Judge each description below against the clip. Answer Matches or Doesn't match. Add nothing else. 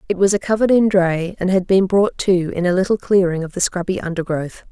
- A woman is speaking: Matches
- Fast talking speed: Matches